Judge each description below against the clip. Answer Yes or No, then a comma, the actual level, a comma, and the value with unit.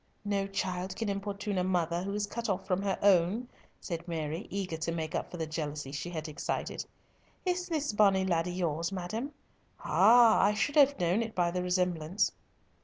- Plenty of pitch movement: No, average, 3.4 semitones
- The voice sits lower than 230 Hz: Yes, medium, 185 Hz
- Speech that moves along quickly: No, average, 185 wpm